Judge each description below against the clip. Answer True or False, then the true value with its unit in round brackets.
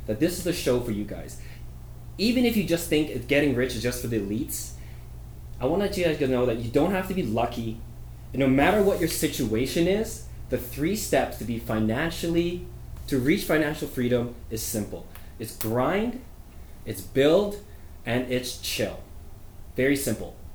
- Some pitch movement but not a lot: False (7.3 semitones)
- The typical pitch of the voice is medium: False (125 Hz)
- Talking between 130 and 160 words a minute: False (180 wpm)